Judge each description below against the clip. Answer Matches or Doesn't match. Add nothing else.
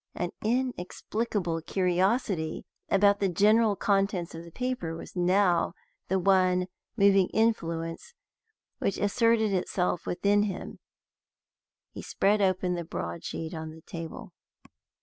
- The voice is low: Doesn't match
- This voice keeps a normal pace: Doesn't match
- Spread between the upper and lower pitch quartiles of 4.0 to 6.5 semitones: Doesn't match